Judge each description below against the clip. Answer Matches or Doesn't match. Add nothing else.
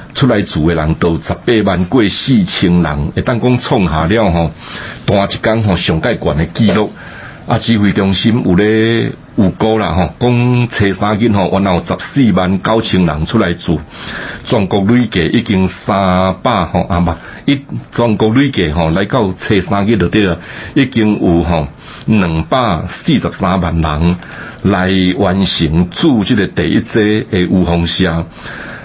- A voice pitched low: Matches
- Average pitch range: Matches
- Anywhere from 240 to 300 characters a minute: Doesn't match